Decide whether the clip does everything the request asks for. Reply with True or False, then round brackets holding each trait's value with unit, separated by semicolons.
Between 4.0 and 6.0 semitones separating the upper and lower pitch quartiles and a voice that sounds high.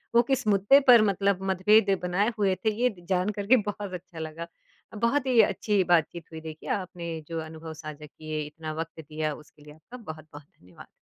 False (4.5 semitones; 175 Hz)